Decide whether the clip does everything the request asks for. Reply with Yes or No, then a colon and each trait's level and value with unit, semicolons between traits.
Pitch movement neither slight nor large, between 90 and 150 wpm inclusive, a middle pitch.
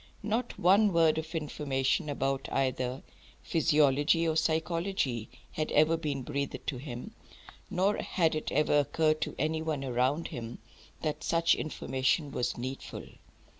Yes: average, 3.4 semitones; slow, 135 wpm; medium, 150 Hz